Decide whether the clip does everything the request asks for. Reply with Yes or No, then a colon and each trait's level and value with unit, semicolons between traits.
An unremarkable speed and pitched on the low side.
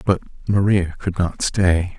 Yes: average, 150 wpm; very low, 95 Hz